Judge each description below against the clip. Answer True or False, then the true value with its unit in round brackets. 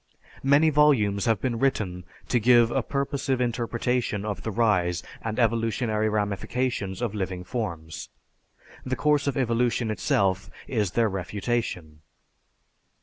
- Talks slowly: True (125 wpm)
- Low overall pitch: True (115 Hz)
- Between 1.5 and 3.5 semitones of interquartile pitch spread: False (3.9 semitones)